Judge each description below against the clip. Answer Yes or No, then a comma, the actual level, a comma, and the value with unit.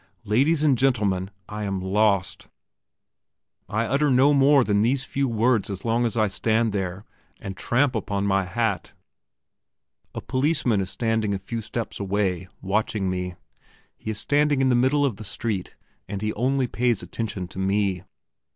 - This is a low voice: Yes, low, 110 Hz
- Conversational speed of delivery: Yes, average, 165 wpm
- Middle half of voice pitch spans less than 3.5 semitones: No, average, 4.5 semitones